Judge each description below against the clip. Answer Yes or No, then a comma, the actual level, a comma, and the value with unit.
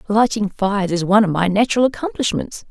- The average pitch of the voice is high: Yes, high, 210 Hz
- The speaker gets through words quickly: No, average, 175 wpm